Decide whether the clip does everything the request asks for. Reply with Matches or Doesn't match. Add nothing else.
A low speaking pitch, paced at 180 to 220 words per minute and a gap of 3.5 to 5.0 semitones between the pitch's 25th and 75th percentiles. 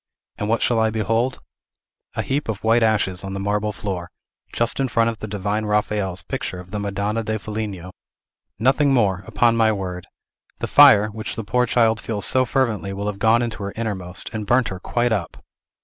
Doesn't match